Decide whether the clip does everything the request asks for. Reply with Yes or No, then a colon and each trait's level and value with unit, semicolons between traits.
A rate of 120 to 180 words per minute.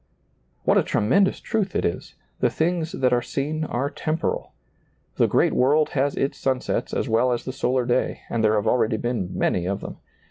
No: average, 190 wpm